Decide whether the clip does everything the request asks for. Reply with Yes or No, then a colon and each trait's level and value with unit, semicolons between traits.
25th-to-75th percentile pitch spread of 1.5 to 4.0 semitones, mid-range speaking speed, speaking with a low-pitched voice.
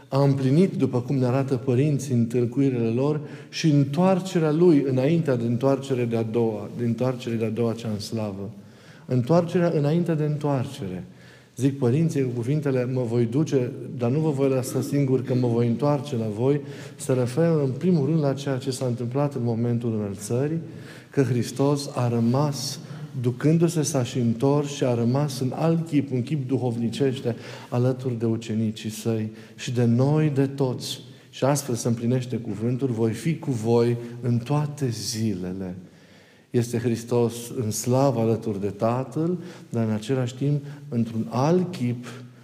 Yes: average, 3.3 semitones; average, 155 wpm; low, 130 Hz